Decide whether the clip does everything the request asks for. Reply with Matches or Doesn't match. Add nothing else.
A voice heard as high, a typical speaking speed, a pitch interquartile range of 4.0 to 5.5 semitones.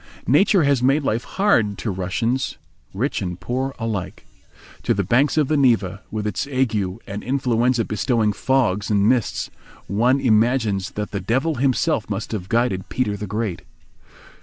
Doesn't match